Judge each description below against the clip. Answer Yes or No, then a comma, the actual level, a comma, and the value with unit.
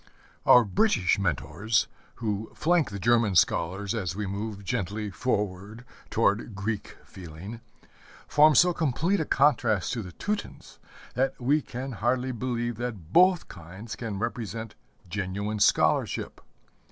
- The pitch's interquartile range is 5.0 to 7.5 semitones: No, average, 4.0 semitones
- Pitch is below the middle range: Yes, low, 110 Hz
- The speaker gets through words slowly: Yes, slow, 125 wpm